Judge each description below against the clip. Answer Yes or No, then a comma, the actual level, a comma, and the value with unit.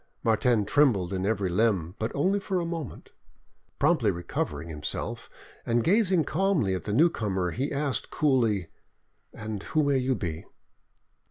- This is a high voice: No, low, 115 Hz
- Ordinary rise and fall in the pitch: No, wide, 7.8 semitones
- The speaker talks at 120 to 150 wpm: Yes, average, 145 wpm